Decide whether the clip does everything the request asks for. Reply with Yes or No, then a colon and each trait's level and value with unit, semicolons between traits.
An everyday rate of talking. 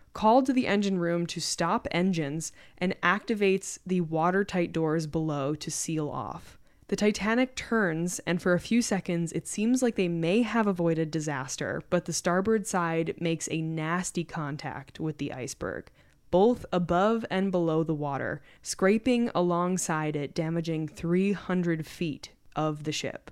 Yes: average, 150 wpm